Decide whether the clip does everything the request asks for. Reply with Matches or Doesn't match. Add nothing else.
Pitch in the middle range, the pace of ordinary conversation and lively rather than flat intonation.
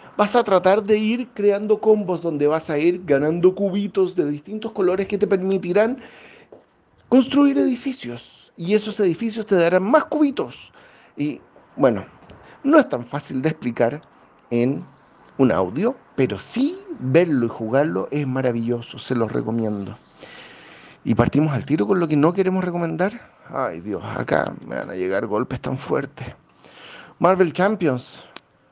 Matches